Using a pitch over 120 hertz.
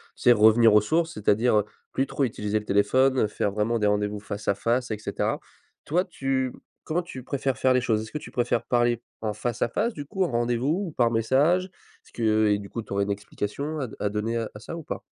No: low, 115 Hz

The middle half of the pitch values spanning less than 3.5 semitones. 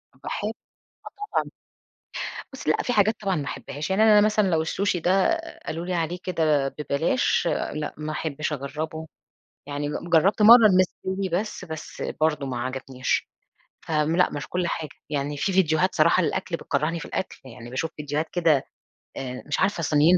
No: average, 4.2 semitones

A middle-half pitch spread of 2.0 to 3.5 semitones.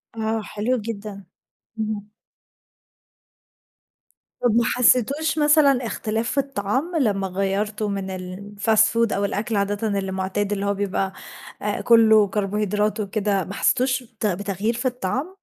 Yes: average, 2.7 semitones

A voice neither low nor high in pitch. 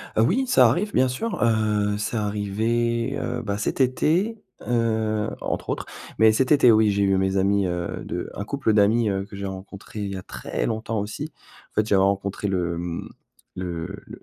No: low, 105 Hz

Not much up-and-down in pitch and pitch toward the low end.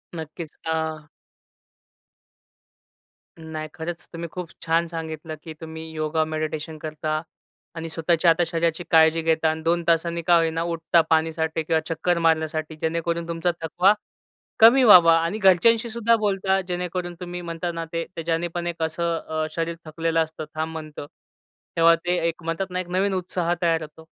No: narrow, 1.4 semitones; medium, 165 Hz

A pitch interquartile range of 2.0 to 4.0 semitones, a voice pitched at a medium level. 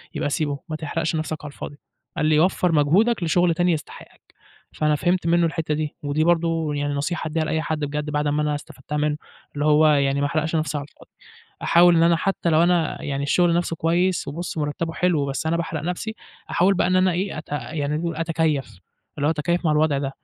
Yes: narrow, 2.4 semitones; medium, 155 Hz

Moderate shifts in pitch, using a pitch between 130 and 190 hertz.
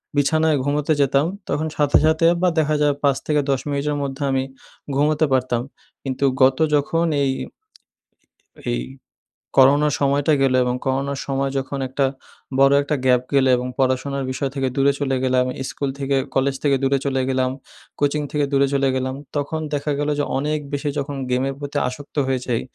No: narrow, 1.5 semitones; medium, 140 Hz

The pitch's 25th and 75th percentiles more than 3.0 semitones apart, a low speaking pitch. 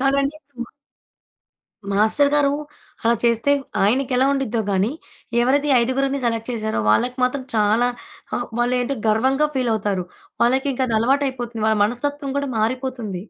No: average, 3.5 semitones; very high, 250 Hz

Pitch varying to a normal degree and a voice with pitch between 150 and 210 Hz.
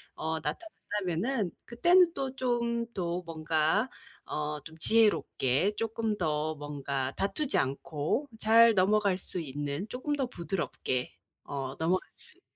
No: wide, 7.3 semitones; medium, 185 Hz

